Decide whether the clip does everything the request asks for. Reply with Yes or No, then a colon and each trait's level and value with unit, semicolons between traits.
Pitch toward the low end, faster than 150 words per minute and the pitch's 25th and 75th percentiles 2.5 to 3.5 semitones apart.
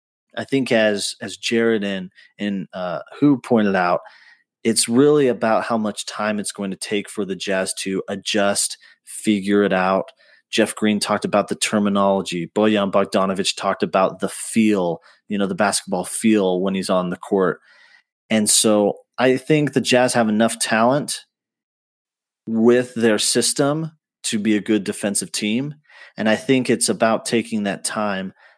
Yes: low, 105 Hz; average, 160 wpm; average, 2.9 semitones